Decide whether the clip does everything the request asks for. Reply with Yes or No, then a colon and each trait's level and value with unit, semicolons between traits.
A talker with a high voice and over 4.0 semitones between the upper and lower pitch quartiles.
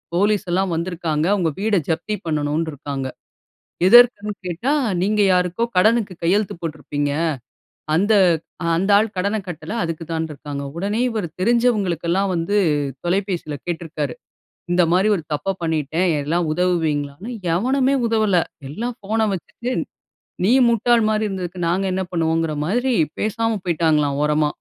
No: medium, 180 Hz; average, 4.7 semitones